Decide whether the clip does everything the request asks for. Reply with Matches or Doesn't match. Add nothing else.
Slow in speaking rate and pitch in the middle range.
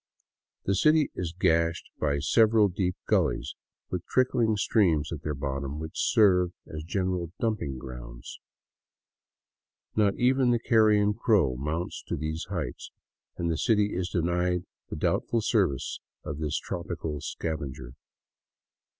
Doesn't match